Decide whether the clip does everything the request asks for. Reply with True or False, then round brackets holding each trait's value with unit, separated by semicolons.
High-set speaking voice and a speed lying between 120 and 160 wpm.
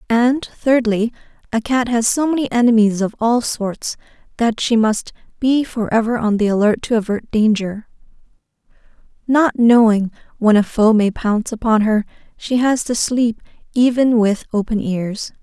True (230 Hz; 155 wpm)